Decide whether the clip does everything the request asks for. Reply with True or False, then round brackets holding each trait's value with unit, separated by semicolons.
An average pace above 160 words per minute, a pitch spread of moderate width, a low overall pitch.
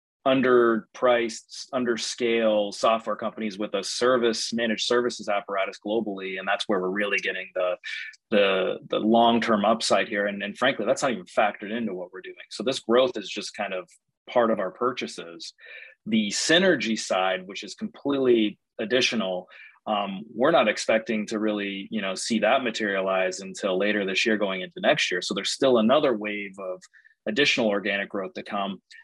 True (170 wpm; 3.0 semitones; 110 Hz)